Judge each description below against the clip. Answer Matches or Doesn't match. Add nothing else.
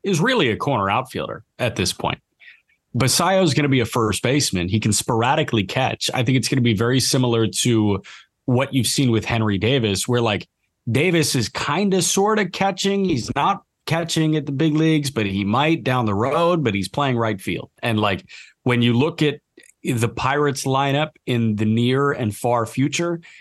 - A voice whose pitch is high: Doesn't match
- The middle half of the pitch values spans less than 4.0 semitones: Doesn't match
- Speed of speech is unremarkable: Matches